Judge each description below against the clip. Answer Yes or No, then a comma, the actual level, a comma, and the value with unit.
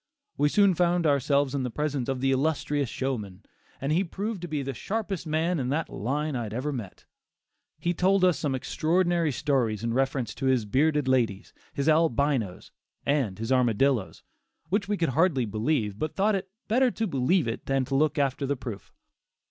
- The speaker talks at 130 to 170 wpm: No, average, 185 wpm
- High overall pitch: No, medium, 140 Hz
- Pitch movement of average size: Yes, average, 4.7 semitones